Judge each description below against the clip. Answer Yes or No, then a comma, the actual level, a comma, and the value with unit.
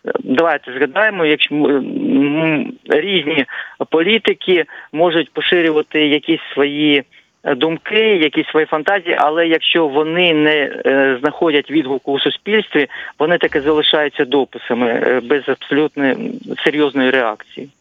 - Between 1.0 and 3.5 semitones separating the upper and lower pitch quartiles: Yes, average, 2.7 semitones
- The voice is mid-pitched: Yes, medium, 150 Hz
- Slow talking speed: Yes, slow, 100 wpm